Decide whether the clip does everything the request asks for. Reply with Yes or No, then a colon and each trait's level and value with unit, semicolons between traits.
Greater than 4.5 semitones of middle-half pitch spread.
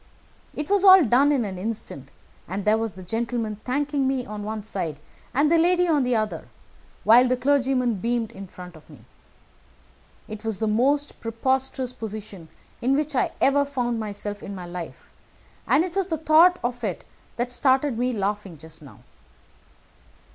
Yes: average, 5.1 semitones